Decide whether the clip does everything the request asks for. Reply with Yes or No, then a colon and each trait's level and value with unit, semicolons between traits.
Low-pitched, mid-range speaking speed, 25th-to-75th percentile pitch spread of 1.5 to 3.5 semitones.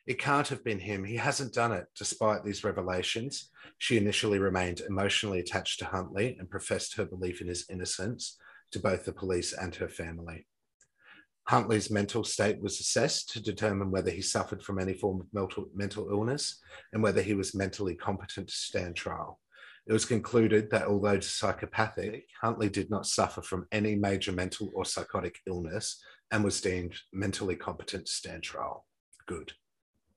Yes: low, 100 Hz; average, 165 wpm; average, 2.7 semitones